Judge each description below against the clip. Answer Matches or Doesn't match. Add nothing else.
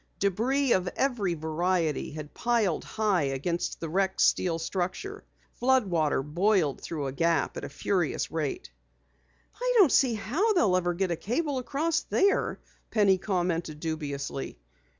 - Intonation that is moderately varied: Doesn't match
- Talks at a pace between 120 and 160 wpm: Matches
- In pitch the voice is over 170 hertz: Matches